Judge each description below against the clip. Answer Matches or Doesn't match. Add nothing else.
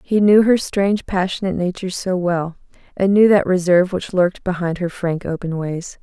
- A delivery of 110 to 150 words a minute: Doesn't match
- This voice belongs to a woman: Matches